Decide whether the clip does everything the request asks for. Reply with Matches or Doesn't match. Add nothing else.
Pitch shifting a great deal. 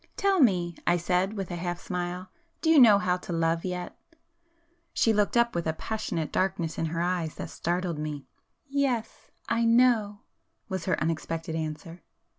Doesn't match